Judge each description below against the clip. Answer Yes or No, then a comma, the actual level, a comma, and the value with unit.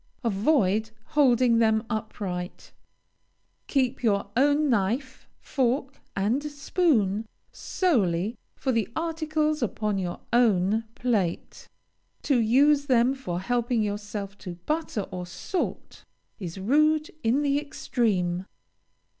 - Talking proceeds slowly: Yes, slow, 105 wpm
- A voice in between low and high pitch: No, high, 235 Hz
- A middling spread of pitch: No, wide, 5.8 semitones